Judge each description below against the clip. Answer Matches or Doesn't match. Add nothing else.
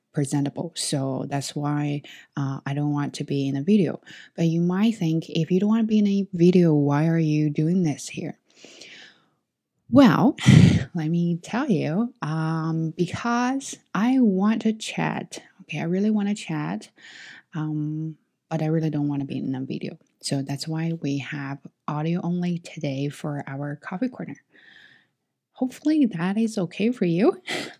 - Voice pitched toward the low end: Doesn't match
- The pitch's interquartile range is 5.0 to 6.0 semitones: Matches